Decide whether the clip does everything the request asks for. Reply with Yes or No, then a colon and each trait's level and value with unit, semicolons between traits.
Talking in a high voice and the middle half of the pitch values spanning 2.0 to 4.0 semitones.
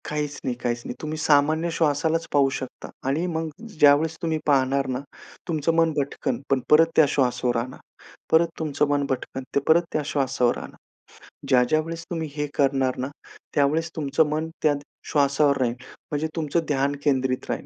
No: medium, 145 Hz; average, 2.8 semitones